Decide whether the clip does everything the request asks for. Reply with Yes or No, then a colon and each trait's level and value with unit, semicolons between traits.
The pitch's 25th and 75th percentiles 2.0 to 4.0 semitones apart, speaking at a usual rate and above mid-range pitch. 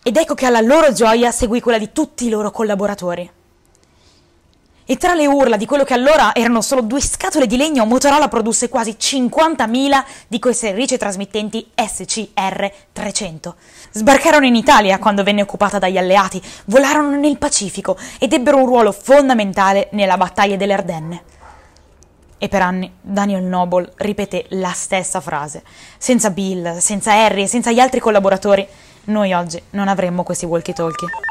No: average, 5.0 semitones; average, 155 wpm; high, 205 Hz